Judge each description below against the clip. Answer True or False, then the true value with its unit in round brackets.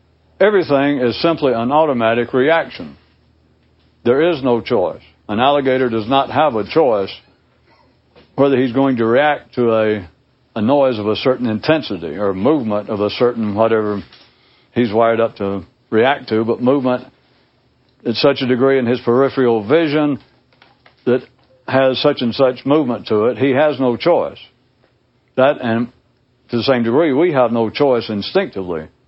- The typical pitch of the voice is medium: False (125 Hz)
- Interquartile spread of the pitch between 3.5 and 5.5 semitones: False (2.9 semitones)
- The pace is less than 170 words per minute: True (155 wpm)